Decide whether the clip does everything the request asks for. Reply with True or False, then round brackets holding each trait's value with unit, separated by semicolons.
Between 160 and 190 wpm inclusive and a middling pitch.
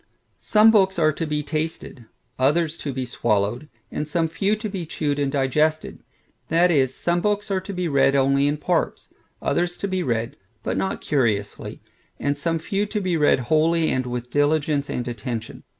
True (180 wpm; 150 Hz)